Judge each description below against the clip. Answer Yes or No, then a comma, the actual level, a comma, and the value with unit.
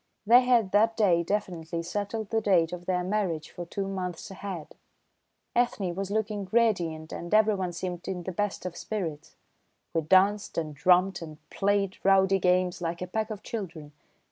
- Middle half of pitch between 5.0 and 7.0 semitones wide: No, average, 3.1 semitones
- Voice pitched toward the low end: No, high, 190 Hz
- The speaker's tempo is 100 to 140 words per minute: No, average, 170 wpm